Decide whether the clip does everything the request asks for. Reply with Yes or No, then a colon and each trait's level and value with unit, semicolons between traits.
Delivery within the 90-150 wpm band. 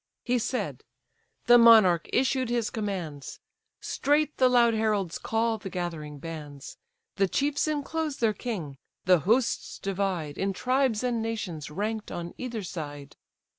Yes: slow, 135 wpm